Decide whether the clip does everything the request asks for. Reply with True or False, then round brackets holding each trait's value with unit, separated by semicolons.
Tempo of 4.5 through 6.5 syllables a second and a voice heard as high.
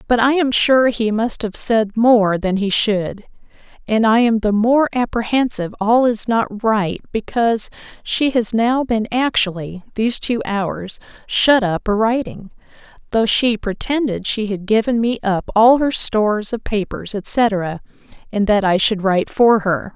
False (4.2 syllables/s; 220 Hz)